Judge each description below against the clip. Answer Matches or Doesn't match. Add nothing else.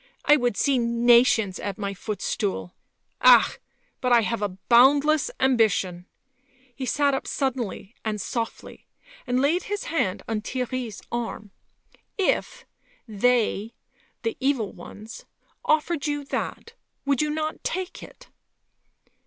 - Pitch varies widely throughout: Doesn't match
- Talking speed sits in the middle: Doesn't match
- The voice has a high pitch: Matches